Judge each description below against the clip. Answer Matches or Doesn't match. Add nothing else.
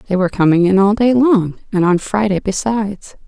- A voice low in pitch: Doesn't match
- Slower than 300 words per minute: Matches